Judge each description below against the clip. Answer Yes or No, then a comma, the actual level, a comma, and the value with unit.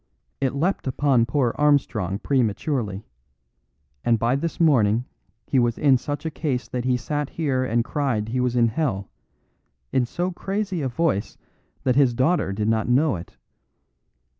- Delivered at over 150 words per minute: Yes, average, 160 wpm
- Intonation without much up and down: No, average, 4.1 semitones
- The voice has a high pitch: No, low, 130 Hz